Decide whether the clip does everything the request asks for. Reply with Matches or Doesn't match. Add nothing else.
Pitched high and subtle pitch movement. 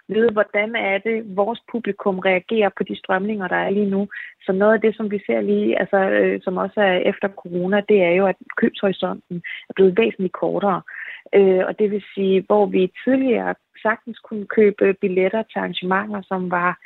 Matches